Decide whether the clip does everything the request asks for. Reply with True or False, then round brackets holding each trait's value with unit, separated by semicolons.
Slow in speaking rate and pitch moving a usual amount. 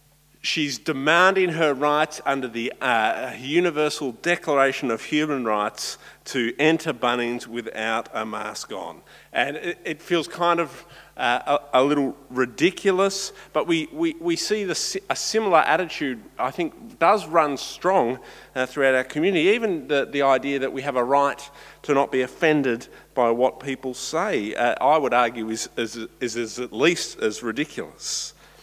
False (160 wpm; 4.6 semitones)